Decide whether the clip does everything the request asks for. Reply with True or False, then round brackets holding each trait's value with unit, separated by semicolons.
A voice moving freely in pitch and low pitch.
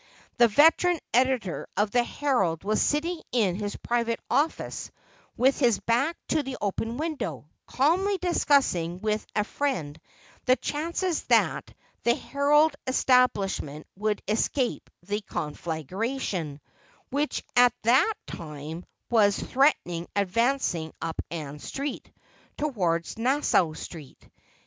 False (8.0 semitones; 235 Hz)